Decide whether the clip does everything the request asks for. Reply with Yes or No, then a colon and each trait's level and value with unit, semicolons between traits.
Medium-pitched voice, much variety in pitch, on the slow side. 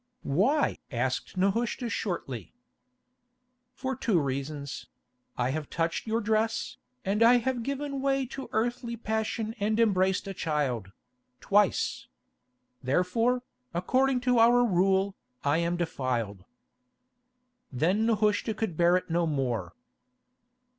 No: high, 195 Hz; wide, 7.5 semitones; slow, 115 wpm